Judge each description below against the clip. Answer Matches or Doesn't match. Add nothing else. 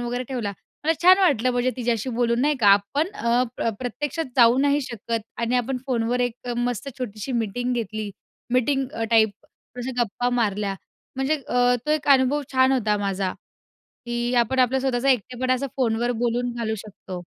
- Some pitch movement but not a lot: Doesn't match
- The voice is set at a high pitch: Matches